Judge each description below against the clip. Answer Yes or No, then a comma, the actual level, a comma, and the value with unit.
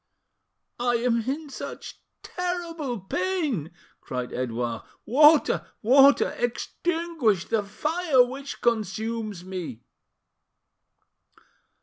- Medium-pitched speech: No, high, 245 Hz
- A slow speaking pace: Yes, slow, 80 wpm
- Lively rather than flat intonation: Yes, wide, 7.2 semitones